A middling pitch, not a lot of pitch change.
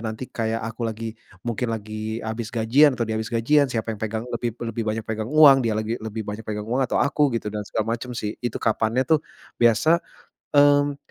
No: low, 115 Hz; narrow, 2.3 semitones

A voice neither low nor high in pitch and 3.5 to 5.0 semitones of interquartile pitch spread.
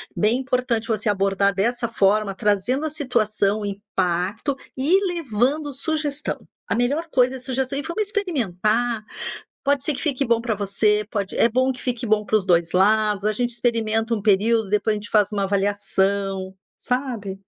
No: high, 220 Hz; average, 4.2 semitones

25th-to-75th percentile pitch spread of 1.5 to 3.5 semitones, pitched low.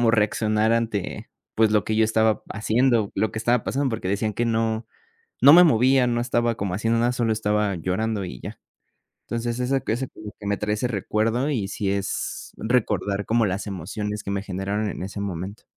Yes: narrow, 2.5 semitones; low, 110 Hz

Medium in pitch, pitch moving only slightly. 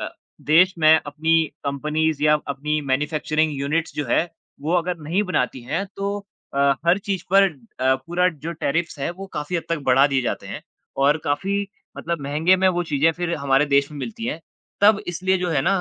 No: medium, 160 Hz; average, 3.7 semitones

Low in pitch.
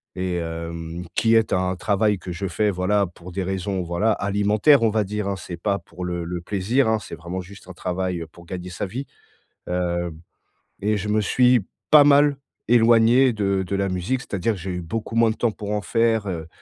Yes: low, 100 Hz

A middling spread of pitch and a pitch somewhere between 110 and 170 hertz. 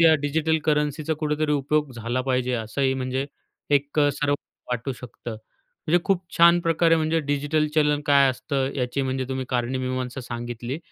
Yes: average, 3.1 semitones; medium, 140 Hz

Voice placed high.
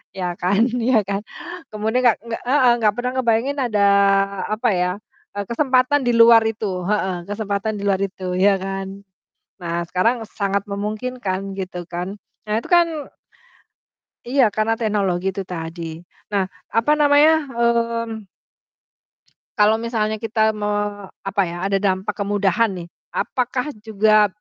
Yes: high, 215 Hz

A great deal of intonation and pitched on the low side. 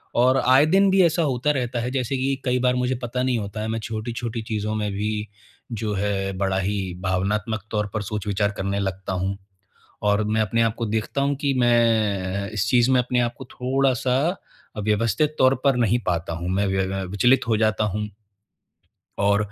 No: average, 3.8 semitones; low, 110 Hz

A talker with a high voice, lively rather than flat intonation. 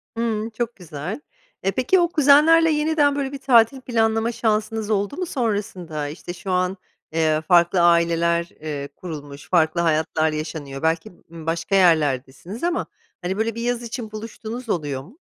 Yes: high, 195 Hz; wide, 6.4 semitones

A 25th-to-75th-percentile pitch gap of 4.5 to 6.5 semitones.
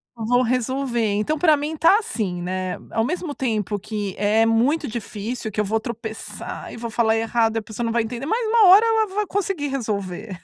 Yes: average, 5.2 semitones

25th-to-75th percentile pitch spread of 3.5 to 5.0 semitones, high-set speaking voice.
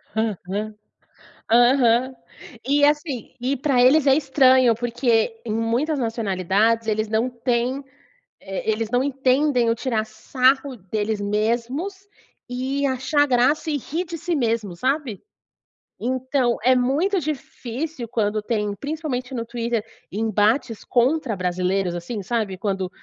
Yes: average, 3.8 semitones; high, 245 Hz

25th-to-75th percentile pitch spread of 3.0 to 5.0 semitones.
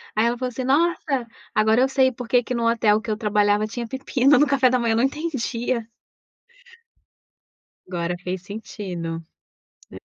Yes: average, 3.6 semitones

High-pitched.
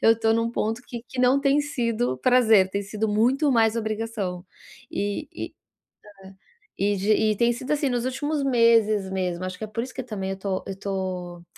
Yes: high, 225 Hz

